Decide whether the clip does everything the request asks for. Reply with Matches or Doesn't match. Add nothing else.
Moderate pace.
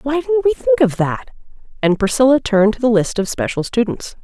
Doesn't match